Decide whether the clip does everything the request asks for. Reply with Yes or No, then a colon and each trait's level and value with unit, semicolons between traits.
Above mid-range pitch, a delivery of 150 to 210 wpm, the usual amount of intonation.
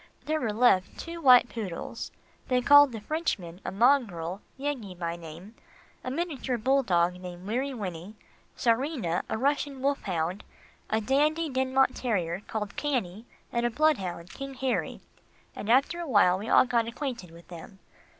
No: high, 235 Hz; average, 160 wpm; wide, 6.7 semitones